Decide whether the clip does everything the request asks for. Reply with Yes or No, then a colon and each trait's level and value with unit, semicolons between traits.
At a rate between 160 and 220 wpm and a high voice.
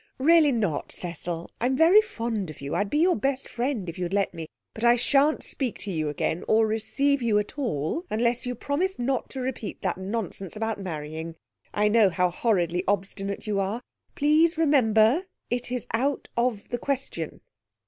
Yes: average, 180 wpm; high, 225 Hz